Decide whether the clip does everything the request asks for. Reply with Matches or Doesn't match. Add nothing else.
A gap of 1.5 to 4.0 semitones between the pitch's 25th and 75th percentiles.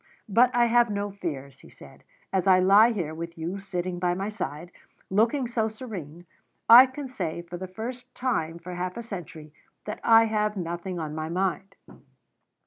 Doesn't match